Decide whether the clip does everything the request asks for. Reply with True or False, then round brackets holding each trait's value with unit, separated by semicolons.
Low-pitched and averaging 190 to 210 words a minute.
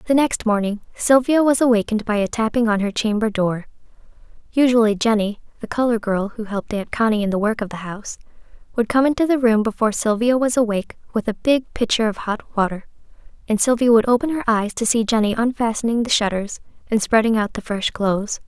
False (225 Hz; 200 wpm)